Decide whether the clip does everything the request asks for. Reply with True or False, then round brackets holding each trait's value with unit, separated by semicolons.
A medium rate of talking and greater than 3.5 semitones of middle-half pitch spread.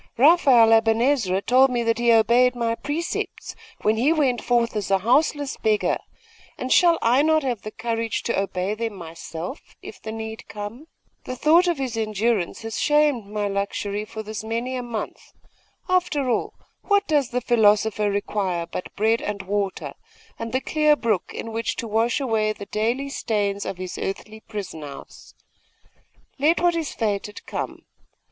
True (165 wpm; 3.9 semitones)